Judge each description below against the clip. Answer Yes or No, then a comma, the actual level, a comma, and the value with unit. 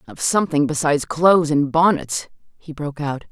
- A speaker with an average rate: Yes, average, 165 wpm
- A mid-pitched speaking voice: Yes, medium, 155 Hz